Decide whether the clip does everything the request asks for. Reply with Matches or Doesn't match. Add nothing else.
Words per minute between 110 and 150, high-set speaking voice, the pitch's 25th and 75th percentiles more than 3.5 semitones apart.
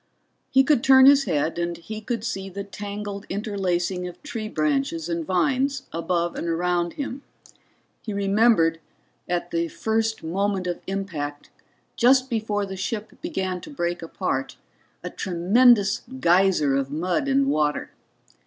Matches